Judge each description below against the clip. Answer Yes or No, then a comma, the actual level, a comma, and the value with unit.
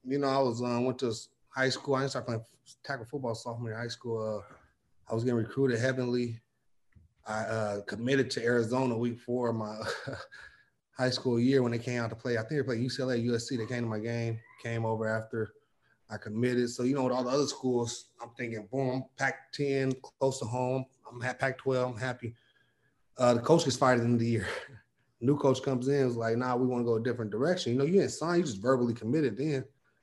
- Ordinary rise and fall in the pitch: No, narrow, 2.2 semitones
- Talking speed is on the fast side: Yes, fast, 230 wpm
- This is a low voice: Yes, low, 125 Hz